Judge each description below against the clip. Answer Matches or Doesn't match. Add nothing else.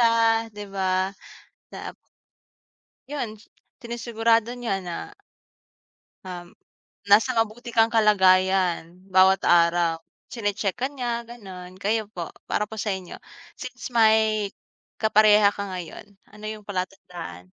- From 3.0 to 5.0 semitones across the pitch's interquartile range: Matches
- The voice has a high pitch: Matches